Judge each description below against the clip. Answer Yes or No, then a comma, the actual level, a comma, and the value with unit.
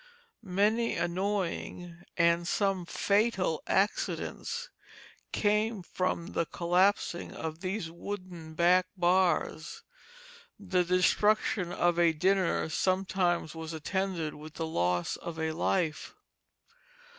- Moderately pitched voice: Yes, medium, 180 Hz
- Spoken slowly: Yes, slow, 100 wpm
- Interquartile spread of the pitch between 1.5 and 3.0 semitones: Yes, average, 2.7 semitones